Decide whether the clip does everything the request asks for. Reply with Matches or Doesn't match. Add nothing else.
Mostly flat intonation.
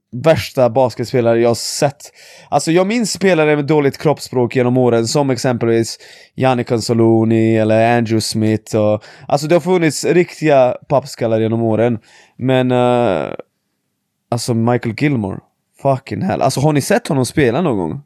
Doesn't match